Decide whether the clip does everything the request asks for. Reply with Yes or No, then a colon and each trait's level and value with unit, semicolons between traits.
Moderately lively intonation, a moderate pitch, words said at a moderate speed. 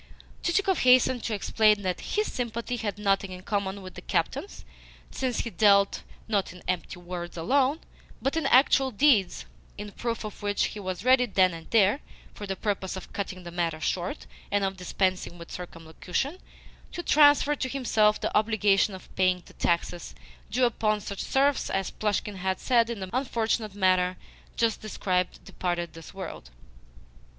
No: average, 4.3 semitones; high, 205 Hz; average, 165 wpm